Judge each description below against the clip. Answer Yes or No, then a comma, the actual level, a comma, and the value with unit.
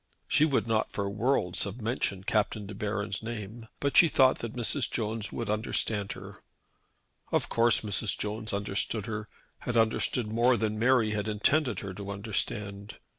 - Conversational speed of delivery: Yes, average, 165 wpm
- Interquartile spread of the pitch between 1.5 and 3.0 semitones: Yes, narrow, 2.4 semitones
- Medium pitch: No, low, 110 Hz